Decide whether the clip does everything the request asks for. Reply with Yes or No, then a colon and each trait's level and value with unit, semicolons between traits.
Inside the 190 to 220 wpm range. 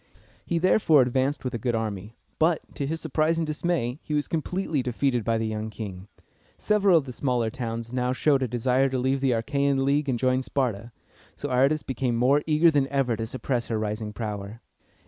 Yes: average, 200 wpm